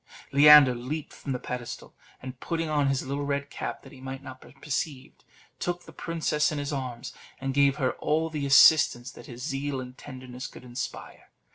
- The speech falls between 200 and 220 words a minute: No, average, 190 wpm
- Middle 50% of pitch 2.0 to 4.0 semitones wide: Yes, narrow, 2.6 semitones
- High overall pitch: No, medium, 140 Hz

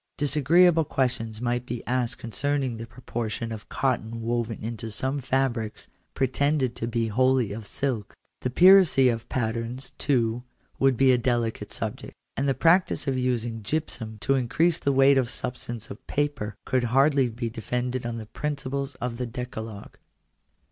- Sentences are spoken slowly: No, average, 155 wpm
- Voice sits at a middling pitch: No, low, 125 Hz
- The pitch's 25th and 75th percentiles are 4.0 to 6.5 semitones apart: No, average, 2.8 semitones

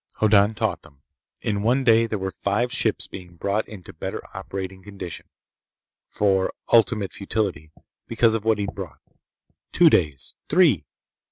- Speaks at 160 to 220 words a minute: No, slow, 135 wpm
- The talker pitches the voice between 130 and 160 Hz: No, low, 100 Hz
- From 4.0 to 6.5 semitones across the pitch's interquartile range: No, average, 2.9 semitones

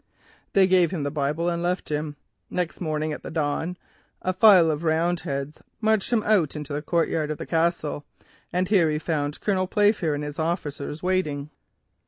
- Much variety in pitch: No, average, 3.4 semitones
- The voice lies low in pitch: No, medium, 165 Hz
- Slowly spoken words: No, average, 175 wpm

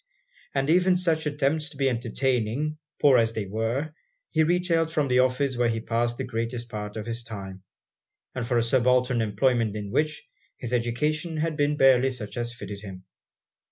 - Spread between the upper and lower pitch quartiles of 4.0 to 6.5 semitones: Yes, average, 4.6 semitones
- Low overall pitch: Yes, low, 125 Hz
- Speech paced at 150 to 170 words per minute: No, average, 180 wpm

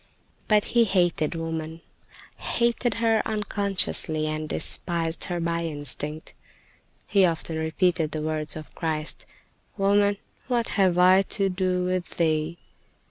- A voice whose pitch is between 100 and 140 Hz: No, medium, 175 Hz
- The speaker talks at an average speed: No, slow, 120 wpm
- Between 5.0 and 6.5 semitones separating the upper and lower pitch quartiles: No, average, 3.8 semitones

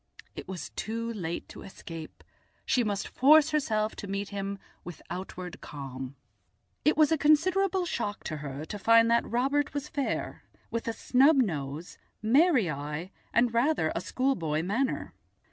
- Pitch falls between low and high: No, high, 220 Hz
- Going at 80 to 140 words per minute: No, average, 155 wpm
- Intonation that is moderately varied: No, wide, 8.0 semitones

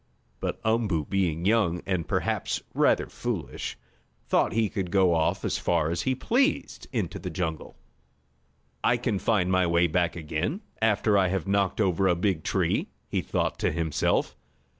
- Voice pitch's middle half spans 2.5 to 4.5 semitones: Yes, average, 3.8 semitones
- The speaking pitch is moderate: No, very low, 95 Hz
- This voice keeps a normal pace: Yes, average, 160 wpm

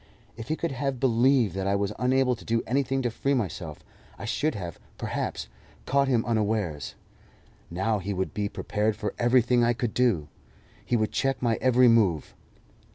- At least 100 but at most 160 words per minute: No, average, 175 wpm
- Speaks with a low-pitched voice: Yes, low, 115 Hz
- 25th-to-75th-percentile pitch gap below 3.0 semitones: No, average, 3.9 semitones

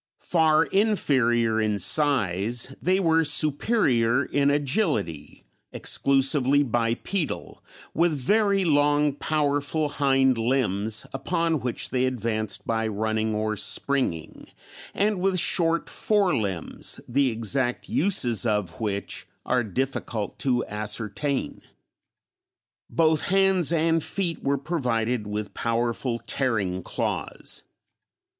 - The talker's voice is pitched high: No, low, 135 Hz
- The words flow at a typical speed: No, slow, 105 wpm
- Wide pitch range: Yes, wide, 5.9 semitones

